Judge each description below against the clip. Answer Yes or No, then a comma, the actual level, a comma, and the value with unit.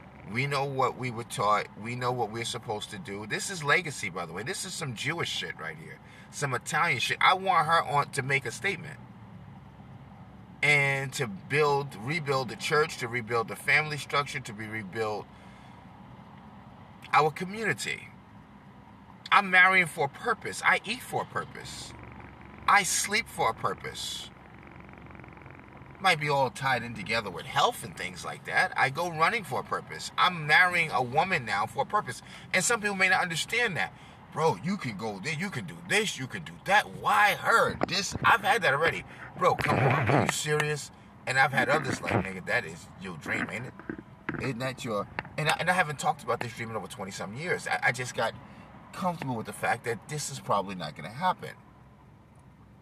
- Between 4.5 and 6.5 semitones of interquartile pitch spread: Yes, average, 4.9 semitones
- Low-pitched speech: No, medium, 145 Hz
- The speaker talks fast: No, average, 195 wpm